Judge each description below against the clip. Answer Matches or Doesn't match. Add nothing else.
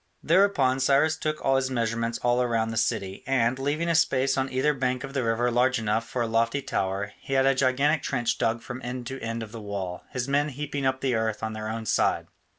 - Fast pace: Matches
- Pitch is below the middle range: Matches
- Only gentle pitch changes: Doesn't match